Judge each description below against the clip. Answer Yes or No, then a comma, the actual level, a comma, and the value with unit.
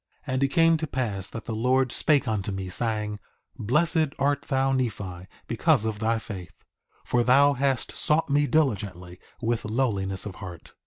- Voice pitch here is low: Yes, low, 120 Hz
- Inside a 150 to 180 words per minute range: Yes, average, 170 wpm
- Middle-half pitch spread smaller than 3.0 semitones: No, average, 5.2 semitones